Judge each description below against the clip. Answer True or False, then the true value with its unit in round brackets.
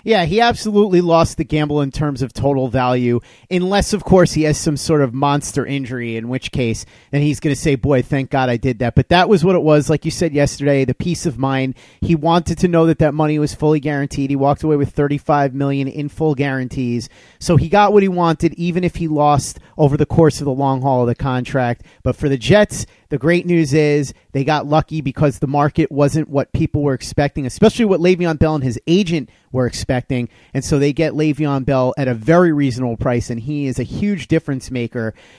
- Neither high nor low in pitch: True (145 Hz)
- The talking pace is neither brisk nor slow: False (225 wpm)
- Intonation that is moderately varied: True (3.4 semitones)